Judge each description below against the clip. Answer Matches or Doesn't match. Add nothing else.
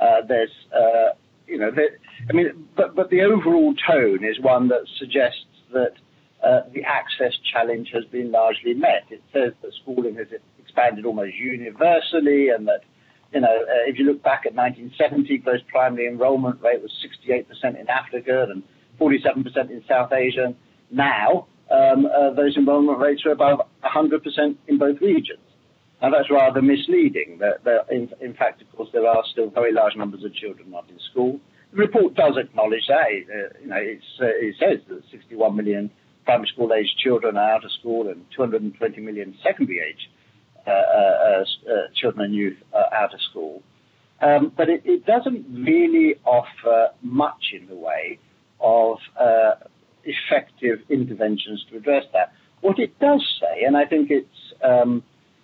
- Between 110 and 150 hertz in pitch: Matches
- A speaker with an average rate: Matches